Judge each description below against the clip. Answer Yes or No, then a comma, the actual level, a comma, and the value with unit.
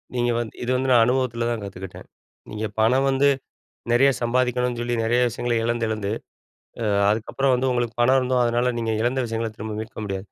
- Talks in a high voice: No, low, 120 Hz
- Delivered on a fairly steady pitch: Yes, narrow, 2.0 semitones